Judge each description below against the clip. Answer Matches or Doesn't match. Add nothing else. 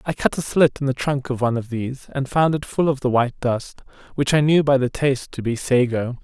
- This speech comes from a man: Matches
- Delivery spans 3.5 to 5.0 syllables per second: Doesn't match